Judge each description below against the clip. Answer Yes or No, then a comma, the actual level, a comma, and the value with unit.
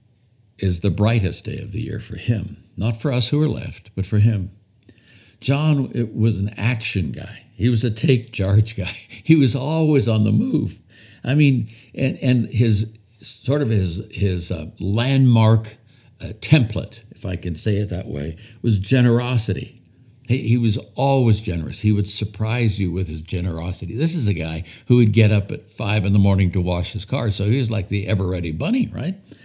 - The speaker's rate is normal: Yes, average, 195 wpm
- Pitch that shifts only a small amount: No, average, 3.2 semitones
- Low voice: Yes, low, 110 Hz